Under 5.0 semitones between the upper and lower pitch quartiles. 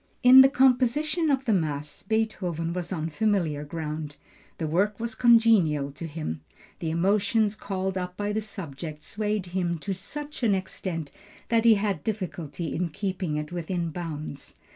No: average, 5.3 semitones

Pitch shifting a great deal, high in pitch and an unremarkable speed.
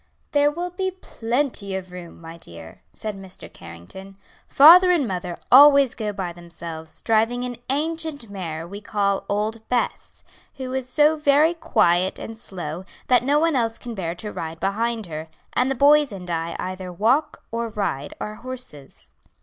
Yes: wide, 7.0 semitones; high, 220 Hz; average, 165 wpm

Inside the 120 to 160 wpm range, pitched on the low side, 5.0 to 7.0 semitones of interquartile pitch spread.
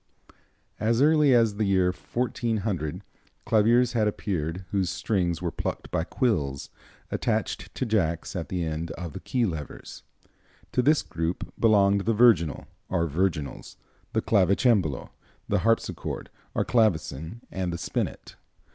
Yes: slow, 135 wpm; very low, 95 Hz; average, 5.3 semitones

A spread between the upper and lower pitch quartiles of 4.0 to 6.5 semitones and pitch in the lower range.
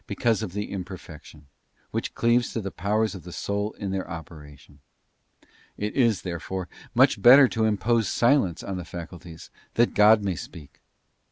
Yes: average, 4.4 semitones; low, 100 Hz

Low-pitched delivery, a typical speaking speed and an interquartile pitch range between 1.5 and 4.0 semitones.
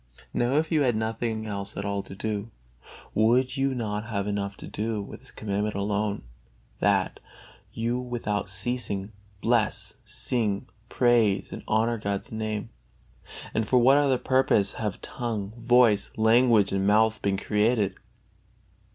Yes: low, 110 Hz; average, 145 wpm; average, 2.9 semitones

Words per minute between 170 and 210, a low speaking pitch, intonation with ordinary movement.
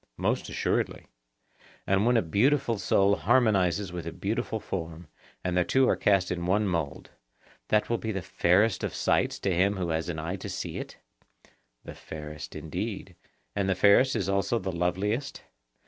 Yes: average, 175 wpm; very low, 95 Hz; average, 3.4 semitones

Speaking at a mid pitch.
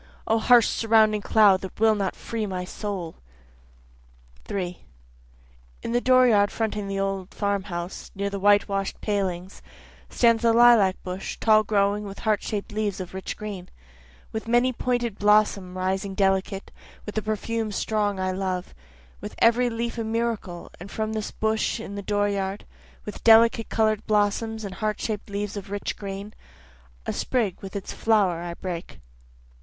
No: high, 205 Hz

